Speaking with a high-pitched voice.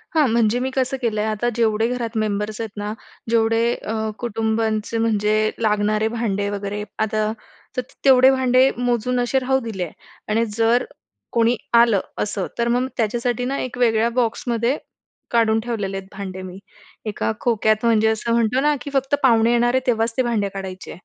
Yes: high, 225 Hz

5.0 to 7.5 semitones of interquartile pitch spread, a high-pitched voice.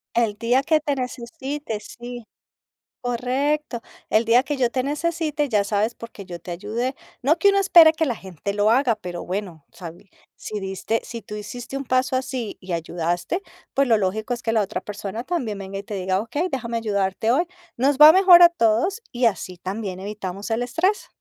Yes: average, 5.3 semitones; high, 230 Hz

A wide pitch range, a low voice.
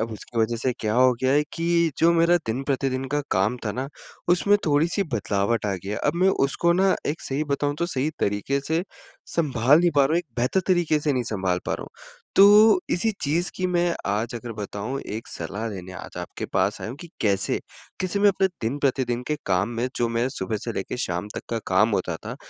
Yes: wide, 7.4 semitones; low, 130 Hz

